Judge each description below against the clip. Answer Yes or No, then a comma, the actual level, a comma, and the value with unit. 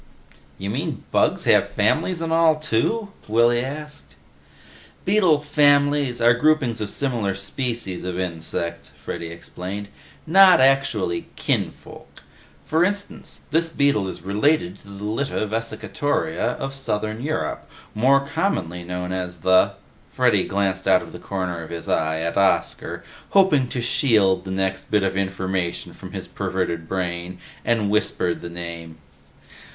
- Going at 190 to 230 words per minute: No, average, 140 wpm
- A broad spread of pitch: Yes, wide, 7.6 semitones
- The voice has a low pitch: Yes, low, 105 Hz